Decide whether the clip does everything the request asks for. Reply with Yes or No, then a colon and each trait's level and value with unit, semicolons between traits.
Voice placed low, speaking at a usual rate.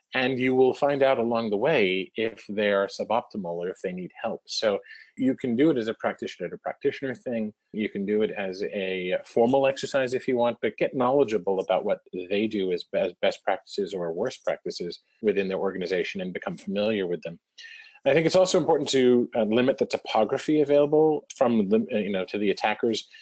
Yes: low, 130 Hz; average, 195 wpm